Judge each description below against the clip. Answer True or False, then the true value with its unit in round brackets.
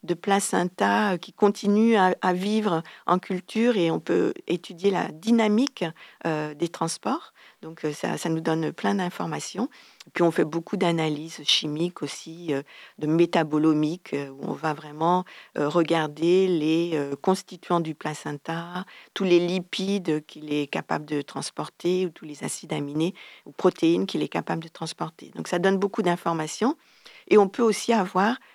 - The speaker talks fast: False (150 wpm)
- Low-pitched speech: False (170 Hz)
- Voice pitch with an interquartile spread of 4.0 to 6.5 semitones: False (3.4 semitones)